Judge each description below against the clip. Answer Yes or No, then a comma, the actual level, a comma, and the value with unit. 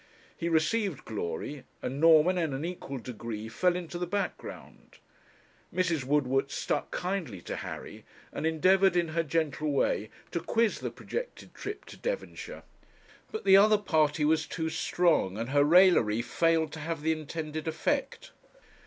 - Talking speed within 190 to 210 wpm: No, average, 155 wpm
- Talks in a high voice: No, medium, 160 Hz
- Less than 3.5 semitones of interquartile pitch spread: No, average, 4.0 semitones